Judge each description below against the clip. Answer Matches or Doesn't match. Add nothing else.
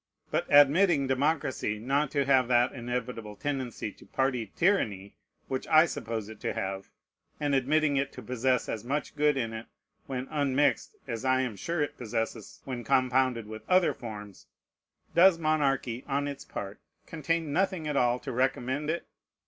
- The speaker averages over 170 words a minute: Doesn't match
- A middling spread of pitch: Matches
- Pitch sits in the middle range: Doesn't match